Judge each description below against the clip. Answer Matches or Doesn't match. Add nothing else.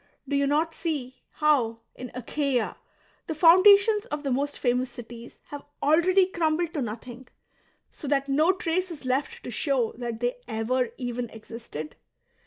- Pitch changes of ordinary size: Matches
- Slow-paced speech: Doesn't match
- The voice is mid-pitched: Doesn't match